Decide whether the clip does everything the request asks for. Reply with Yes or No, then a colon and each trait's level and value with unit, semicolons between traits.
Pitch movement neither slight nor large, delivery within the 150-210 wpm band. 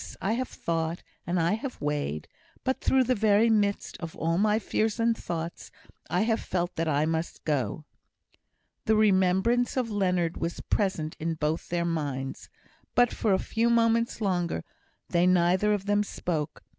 Yes: average, 5.0 semitones; average, 165 wpm